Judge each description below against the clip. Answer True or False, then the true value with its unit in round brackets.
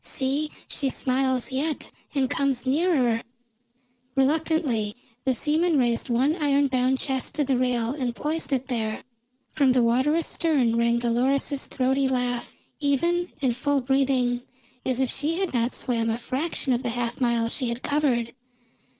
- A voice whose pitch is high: True (260 Hz)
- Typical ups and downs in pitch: True (3.0 semitones)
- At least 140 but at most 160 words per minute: True (155 wpm)